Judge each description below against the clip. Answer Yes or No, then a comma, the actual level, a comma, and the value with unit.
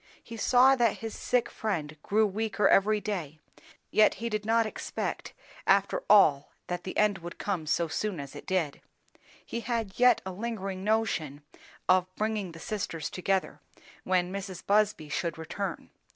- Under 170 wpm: Yes, average, 160 wpm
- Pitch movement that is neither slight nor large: Yes, average, 4.0 semitones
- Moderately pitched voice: No, high, 195 Hz